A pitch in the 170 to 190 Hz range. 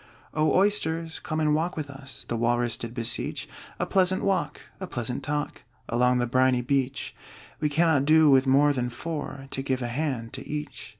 No: medium, 140 Hz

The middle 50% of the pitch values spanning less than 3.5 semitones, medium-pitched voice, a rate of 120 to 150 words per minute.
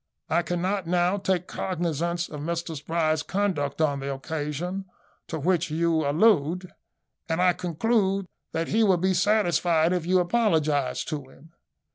Yes: average, 2.9 semitones; medium, 170 Hz; average, 145 wpm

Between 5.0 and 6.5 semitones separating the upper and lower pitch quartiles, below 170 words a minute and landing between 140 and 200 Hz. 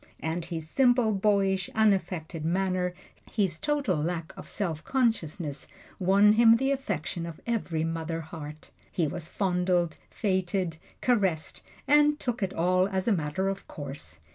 No: average, 4.3 semitones; average, 140 wpm; medium, 185 Hz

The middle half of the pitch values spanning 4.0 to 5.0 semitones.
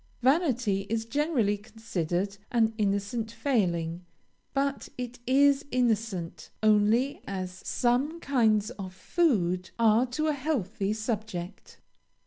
Yes: average, 4.6 semitones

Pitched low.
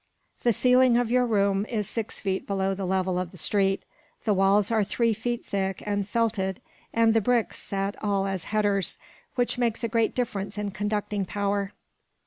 No: high, 205 Hz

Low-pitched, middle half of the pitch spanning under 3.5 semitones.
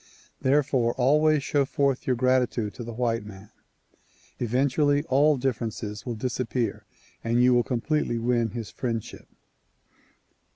Yes: low, 125 Hz; average, 2.9 semitones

